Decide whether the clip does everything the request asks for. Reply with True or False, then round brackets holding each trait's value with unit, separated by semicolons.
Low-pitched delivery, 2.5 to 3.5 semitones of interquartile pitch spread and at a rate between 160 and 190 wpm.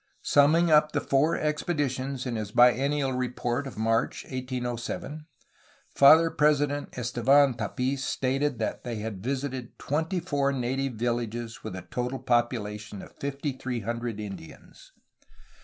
False (130 Hz; 3.2 semitones; 135 wpm)